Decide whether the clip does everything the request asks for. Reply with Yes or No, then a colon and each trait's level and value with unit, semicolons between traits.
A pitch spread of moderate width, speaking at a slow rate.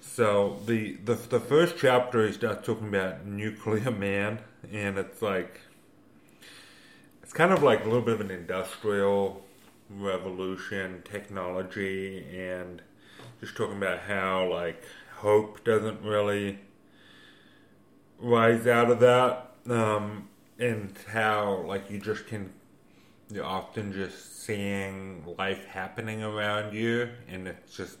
No: narrow, 2.2 semitones; slow, 125 wpm